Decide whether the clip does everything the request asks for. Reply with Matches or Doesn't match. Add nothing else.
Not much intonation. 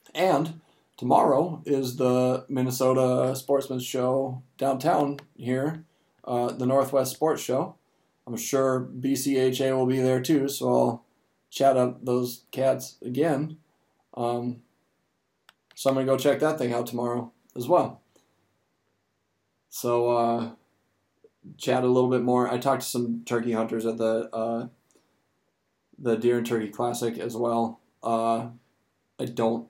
Matches